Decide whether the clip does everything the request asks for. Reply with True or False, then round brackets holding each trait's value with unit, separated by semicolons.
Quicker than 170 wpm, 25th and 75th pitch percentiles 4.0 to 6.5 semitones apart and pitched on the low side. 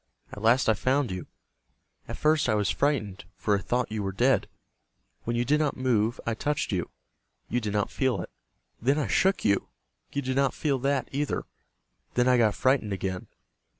True (190 wpm; 4.7 semitones; 125 Hz)